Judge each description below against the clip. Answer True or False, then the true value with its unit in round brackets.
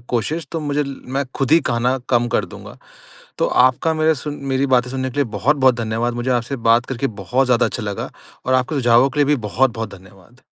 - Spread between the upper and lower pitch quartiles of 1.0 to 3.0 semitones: True (2.7 semitones)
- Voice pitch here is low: True (130 Hz)